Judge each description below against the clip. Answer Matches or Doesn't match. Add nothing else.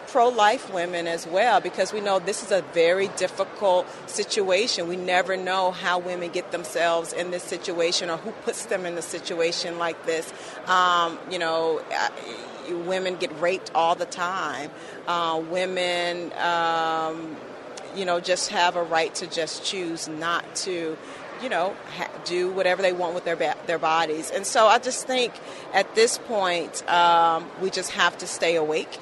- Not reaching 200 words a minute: Matches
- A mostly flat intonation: Matches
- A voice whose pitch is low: Doesn't match